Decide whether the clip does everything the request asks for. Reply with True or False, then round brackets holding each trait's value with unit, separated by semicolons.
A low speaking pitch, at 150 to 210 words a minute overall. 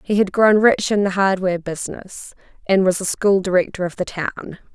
False (190 Hz; 200 wpm)